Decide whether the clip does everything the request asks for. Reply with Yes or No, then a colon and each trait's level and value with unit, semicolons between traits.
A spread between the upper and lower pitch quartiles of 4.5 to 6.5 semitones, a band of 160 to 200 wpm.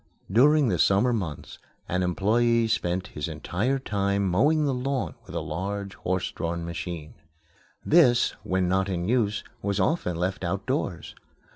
No: average, 5.2 semitones; average, 145 wpm